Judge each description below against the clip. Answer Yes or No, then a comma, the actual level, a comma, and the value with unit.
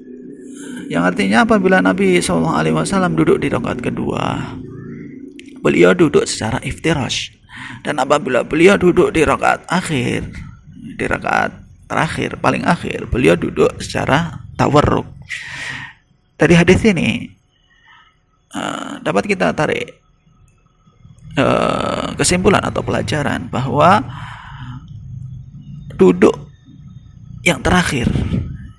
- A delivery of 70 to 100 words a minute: Yes, average, 90 wpm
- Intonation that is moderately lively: No, wide, 6.5 semitones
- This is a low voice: No, medium, 145 Hz